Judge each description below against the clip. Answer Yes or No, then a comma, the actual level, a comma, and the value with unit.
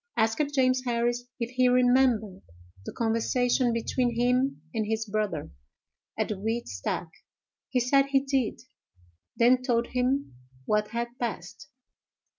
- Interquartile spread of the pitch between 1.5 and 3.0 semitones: Yes, narrow, 2.4 semitones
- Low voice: No, high, 240 Hz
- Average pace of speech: No, slow, 130 wpm